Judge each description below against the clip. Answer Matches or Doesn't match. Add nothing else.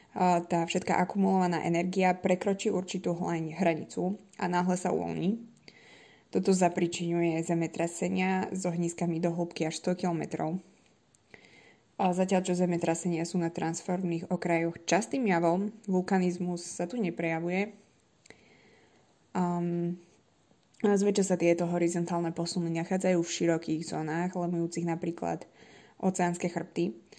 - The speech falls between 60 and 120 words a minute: Matches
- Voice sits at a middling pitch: Matches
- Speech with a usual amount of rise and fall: Doesn't match